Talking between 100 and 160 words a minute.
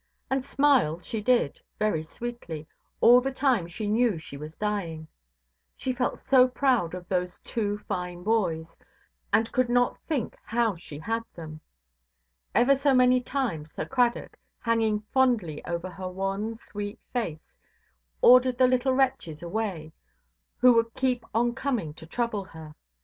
Yes: average, 150 wpm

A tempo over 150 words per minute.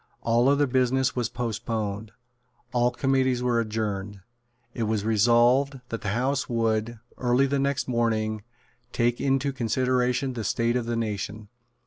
No: average, 140 wpm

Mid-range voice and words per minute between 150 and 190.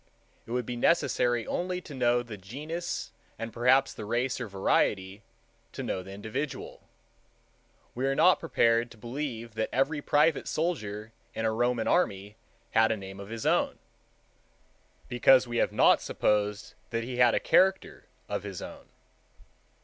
No: low, 120 Hz; average, 155 wpm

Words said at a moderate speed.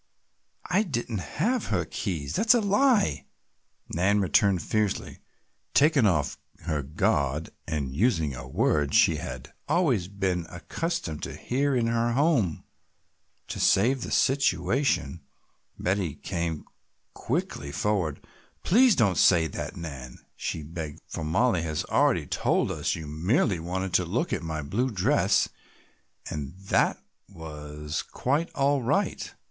No: slow, 130 wpm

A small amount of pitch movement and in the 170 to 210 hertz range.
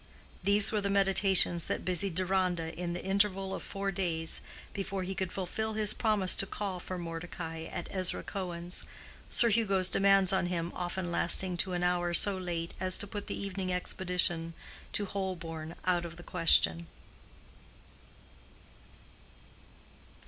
Yes: narrow, 2.2 semitones; medium, 185 Hz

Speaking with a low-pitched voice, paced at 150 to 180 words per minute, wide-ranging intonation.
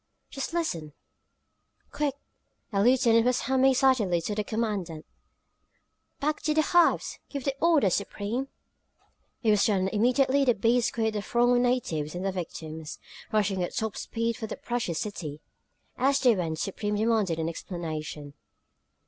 No: high, 220 Hz; average, 155 wpm; wide, 5.8 semitones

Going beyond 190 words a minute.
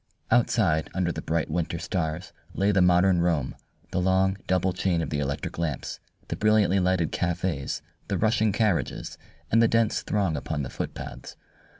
No: average, 165 wpm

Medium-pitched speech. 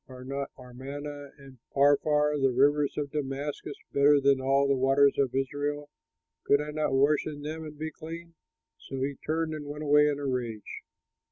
Yes: medium, 145 Hz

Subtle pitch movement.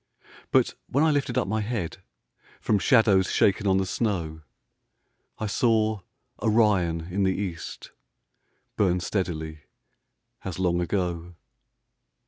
No: average, 3.7 semitones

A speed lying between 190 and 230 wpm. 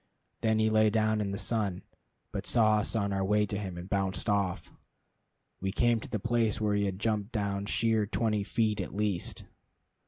Yes: average, 195 wpm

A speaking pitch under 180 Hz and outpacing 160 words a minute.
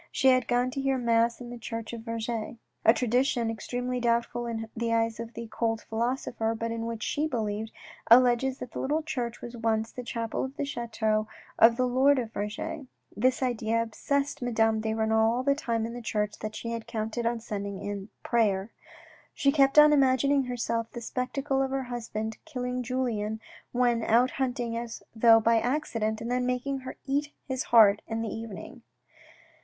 No: high, 235 Hz; average, 190 wpm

